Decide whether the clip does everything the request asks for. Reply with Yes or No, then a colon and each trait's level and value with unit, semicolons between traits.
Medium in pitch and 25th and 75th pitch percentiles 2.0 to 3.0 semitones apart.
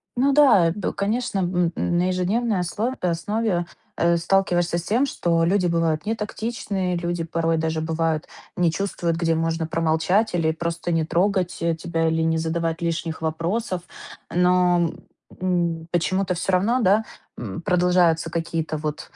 Yes: medium, 175 Hz; narrow, 2.4 semitones